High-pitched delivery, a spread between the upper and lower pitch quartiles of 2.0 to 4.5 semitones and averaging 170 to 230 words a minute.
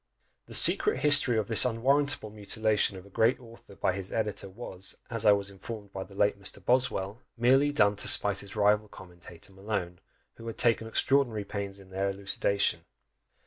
No: low, 105 Hz; average, 2.8 semitones; average, 180 wpm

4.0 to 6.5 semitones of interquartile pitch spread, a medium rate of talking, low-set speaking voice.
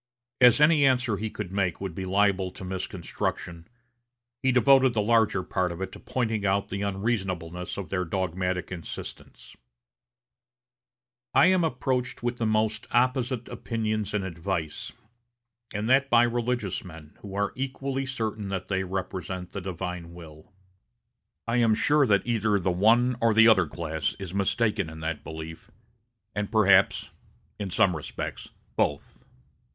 Yes: average, 4.3 semitones; average, 150 wpm; low, 100 Hz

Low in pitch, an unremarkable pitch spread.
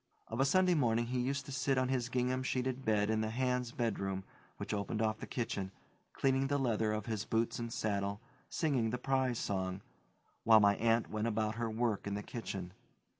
Yes: low, 115 Hz; average, 3.2 semitones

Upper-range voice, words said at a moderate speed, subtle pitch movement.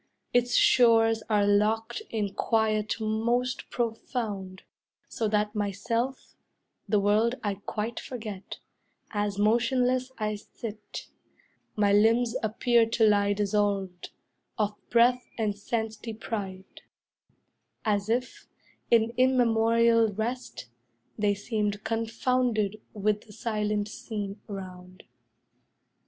No: high, 220 Hz; slow, 100 wpm; narrow, 2.1 semitones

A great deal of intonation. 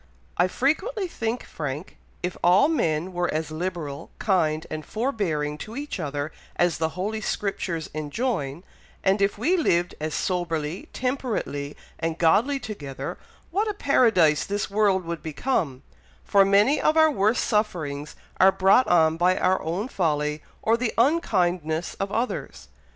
Yes: wide, 6.1 semitones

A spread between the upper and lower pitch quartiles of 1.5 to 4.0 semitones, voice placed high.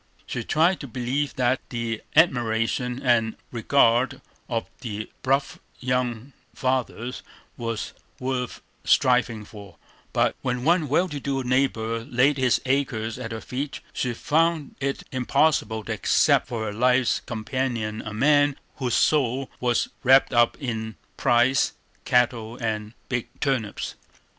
No: average, 2.9 semitones; low, 125 Hz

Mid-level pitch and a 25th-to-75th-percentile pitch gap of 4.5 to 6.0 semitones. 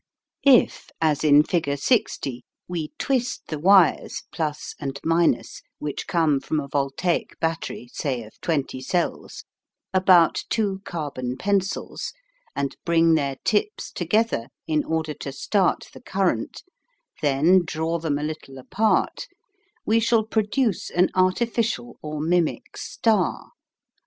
Yes: medium, 165 Hz; average, 5.1 semitones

